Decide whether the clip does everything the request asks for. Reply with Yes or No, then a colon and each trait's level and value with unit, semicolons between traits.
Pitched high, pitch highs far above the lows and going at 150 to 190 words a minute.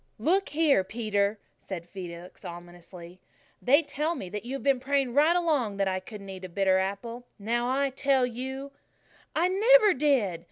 Yes: high, 240 Hz; wide, 6.7 semitones; average, 170 wpm